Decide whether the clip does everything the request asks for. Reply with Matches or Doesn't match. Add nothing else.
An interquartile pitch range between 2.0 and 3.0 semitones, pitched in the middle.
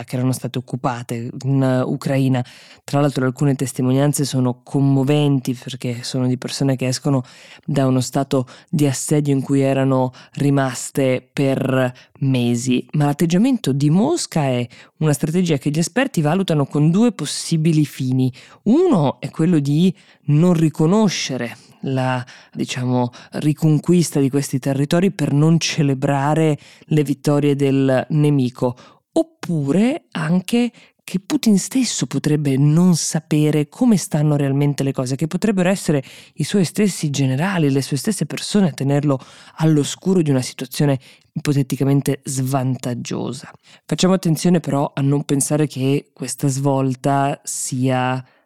Doesn't match